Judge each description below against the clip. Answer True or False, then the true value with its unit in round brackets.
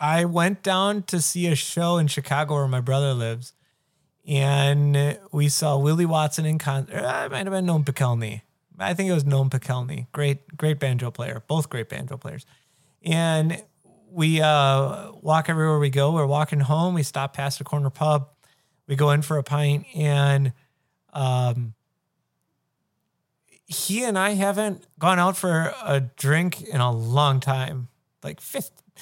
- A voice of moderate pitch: True (145 Hz)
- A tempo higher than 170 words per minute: False (165 wpm)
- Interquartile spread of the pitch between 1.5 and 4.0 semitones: True (2.9 semitones)